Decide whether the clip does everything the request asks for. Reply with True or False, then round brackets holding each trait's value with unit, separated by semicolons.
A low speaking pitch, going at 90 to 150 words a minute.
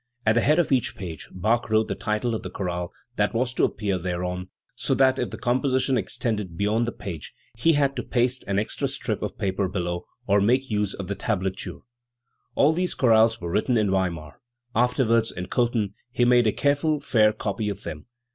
False (110 Hz; 200 wpm)